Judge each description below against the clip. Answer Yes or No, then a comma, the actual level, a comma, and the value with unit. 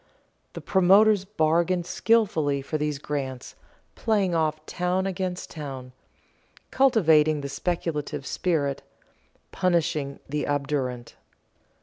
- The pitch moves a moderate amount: Yes, average, 4.2 semitones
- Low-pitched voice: No, medium, 155 Hz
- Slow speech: Yes, slow, 95 wpm